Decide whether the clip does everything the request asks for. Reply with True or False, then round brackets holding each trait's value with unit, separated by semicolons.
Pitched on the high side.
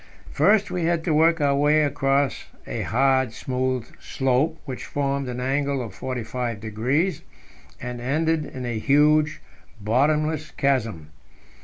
False (135 Hz)